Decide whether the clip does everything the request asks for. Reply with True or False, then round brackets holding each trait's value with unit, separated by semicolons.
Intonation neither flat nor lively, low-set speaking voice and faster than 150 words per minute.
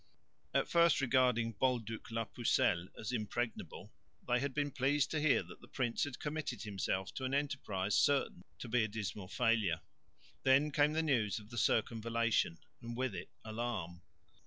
True (3.9 semitones; 120 Hz; 165 wpm)